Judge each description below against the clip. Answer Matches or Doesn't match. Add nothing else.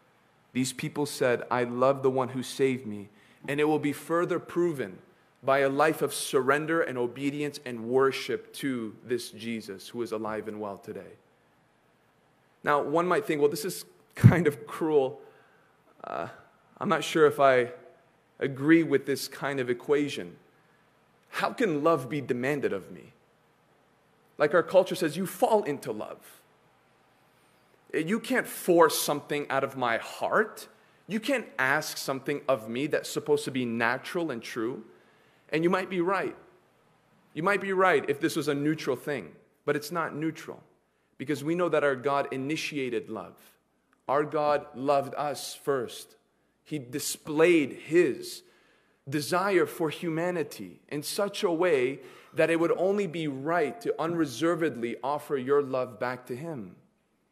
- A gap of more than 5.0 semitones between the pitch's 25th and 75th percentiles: Doesn't match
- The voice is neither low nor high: Matches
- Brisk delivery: Doesn't match